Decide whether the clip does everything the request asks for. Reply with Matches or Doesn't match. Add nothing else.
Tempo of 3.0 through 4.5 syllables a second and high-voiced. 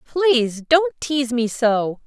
Matches